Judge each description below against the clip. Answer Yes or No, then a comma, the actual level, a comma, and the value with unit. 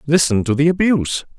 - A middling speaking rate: Yes, average, 175 wpm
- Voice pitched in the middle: Yes, medium, 150 Hz